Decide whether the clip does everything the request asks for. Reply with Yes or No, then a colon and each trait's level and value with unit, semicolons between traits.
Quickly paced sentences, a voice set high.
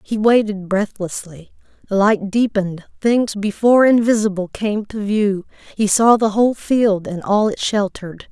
No: average, 150 wpm; high, 210 Hz